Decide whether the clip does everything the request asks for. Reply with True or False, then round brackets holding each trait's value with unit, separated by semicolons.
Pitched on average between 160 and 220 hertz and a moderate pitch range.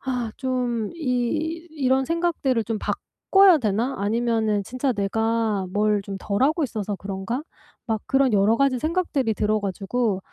False (235 Hz; 4.3 semitones)